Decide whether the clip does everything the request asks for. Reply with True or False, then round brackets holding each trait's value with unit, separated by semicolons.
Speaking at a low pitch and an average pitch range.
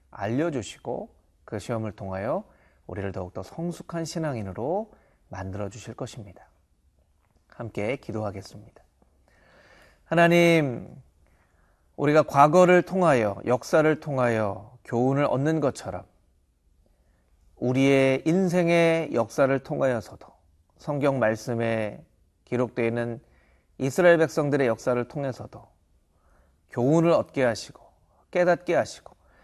False (115 Hz; 8.1 semitones)